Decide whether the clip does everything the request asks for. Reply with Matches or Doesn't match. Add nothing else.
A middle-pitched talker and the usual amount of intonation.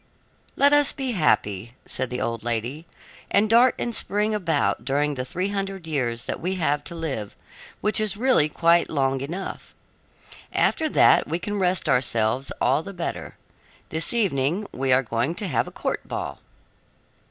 Doesn't match